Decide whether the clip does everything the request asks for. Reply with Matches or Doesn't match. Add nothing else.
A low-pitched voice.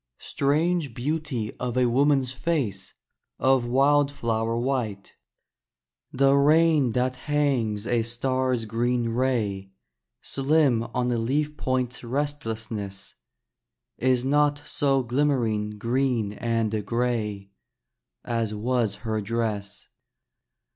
Matches